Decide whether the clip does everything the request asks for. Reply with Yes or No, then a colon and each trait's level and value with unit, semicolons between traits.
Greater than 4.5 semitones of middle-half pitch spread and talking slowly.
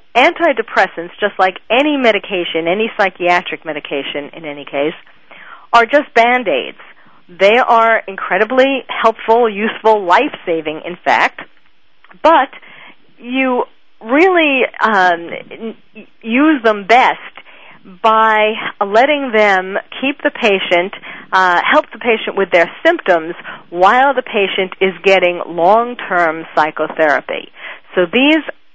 Yes: average, 5.3 semitones; slow, 105 wpm